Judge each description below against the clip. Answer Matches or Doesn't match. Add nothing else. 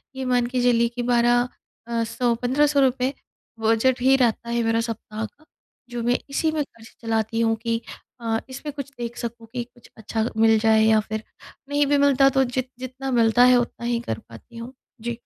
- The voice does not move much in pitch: Matches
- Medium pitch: Doesn't match